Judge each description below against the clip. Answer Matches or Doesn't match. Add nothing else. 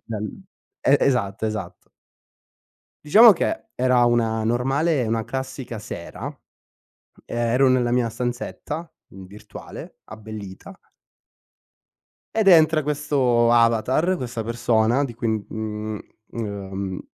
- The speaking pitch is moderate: Doesn't match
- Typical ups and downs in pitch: Matches